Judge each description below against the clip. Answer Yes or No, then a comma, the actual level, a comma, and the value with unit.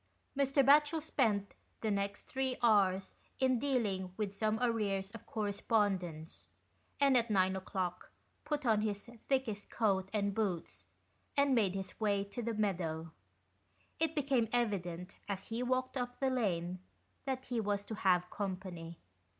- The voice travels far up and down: No, average, 4.5 semitones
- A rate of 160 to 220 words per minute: No, average, 145 wpm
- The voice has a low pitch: No, high, 210 Hz